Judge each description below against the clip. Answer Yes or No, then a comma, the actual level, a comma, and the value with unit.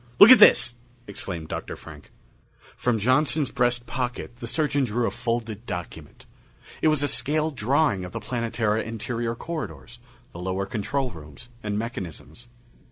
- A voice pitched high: No, low, 120 Hz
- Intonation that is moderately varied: Yes, average, 4.0 semitones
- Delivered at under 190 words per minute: Yes, average, 150 wpm